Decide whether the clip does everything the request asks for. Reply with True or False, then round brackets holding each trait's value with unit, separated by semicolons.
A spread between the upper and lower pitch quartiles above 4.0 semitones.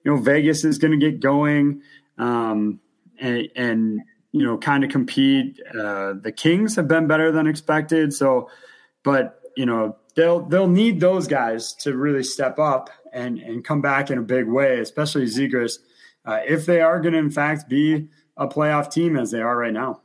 True (4.6 semitones)